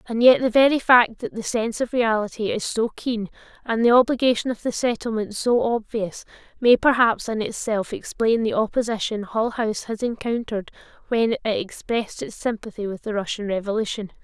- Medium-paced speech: Yes, average, 175 wpm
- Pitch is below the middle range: No, high, 225 Hz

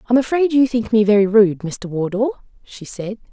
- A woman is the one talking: Yes, female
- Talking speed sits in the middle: No, fast, 215 wpm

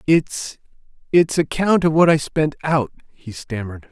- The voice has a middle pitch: Yes, medium, 145 Hz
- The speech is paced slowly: Yes, slow, 125 wpm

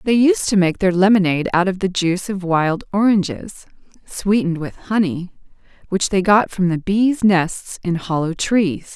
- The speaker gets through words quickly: No, average, 175 wpm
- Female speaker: Yes, female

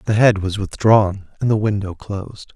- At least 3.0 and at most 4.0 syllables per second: No, 4.8 syllables/s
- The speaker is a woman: No, male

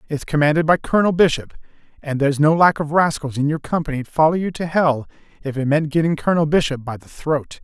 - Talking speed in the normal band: No, fast, 210 wpm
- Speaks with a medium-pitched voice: Yes, medium, 150 Hz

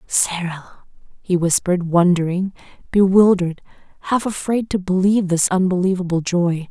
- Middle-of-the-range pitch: Yes, medium, 180 Hz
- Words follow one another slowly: Yes, slow, 105 wpm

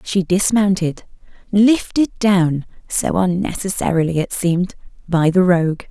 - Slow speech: Yes, slow, 100 wpm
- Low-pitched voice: No, medium, 185 Hz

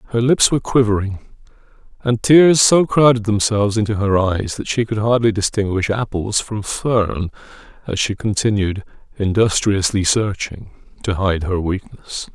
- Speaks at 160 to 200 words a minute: No, average, 140 wpm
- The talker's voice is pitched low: Yes, low, 105 Hz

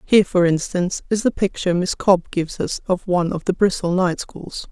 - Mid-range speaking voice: Yes, medium, 180 Hz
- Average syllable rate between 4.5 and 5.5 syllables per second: No, 5.9 syllables/s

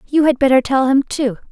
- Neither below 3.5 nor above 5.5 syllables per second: No, 5.7 syllables/s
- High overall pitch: Yes, very high, 265 Hz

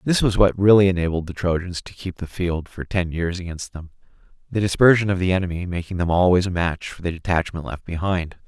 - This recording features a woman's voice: No, male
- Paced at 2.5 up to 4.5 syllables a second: No, 5.8 syllables/s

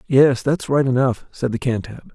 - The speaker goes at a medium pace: Yes, average, 195 wpm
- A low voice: Yes, low, 130 Hz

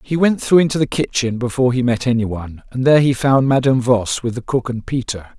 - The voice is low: Yes, low, 125 Hz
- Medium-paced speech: No, fast, 245 wpm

